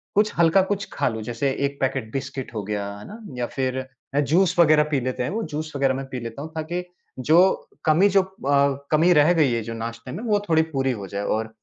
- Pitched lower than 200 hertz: Yes, medium, 140 Hz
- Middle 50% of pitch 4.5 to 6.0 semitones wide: Yes, average, 5.1 semitones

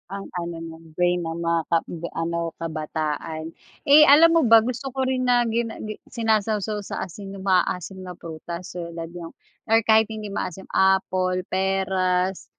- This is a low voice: No, medium, 185 Hz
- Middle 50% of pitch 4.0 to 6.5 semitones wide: Yes, average, 4.3 semitones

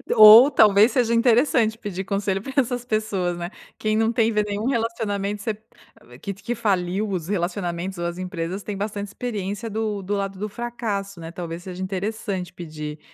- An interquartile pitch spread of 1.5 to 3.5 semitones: Yes, average, 3.1 semitones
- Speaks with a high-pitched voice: Yes, high, 205 Hz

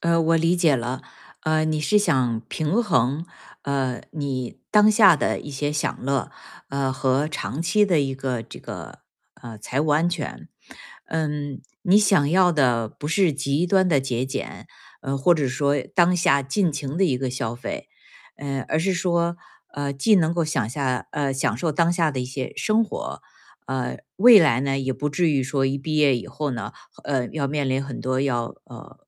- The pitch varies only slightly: No, average, 4.0 semitones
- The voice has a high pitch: No, medium, 145 Hz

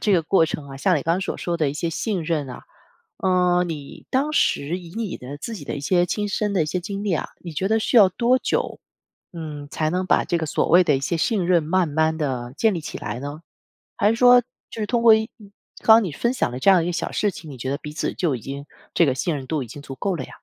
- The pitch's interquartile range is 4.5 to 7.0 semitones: Yes, average, 5.1 semitones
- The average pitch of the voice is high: No, medium, 170 Hz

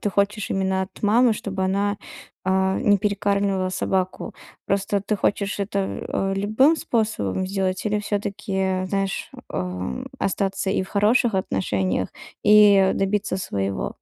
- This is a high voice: Yes, high, 195 Hz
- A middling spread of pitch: No, narrow, 1.5 semitones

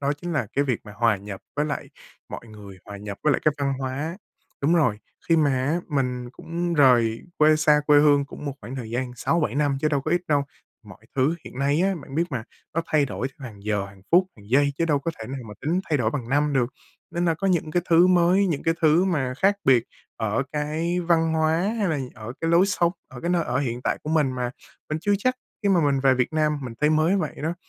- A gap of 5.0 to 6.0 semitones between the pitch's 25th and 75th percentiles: No, average, 4.6 semitones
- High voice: No, medium, 145 Hz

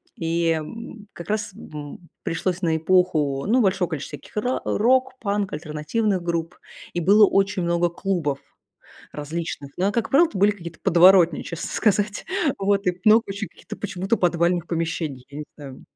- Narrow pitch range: No, average, 3.8 semitones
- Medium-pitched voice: Yes, medium, 180 Hz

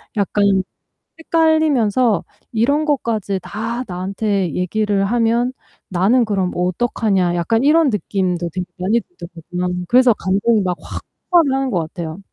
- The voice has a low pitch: No, high, 205 Hz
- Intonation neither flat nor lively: Yes, average, 4.9 semitones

